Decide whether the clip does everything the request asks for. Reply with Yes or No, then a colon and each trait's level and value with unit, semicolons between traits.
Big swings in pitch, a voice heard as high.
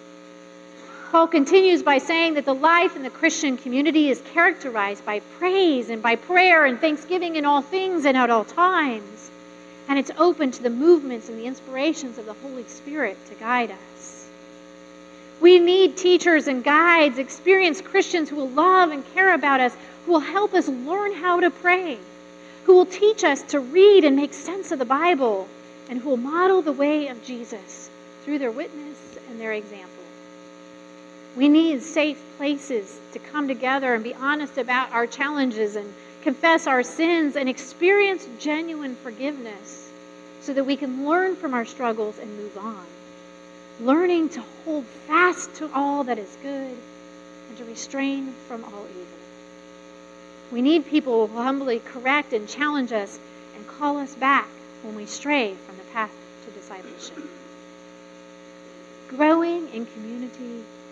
Yes: wide, 8.1 semitones; very high, 270 Hz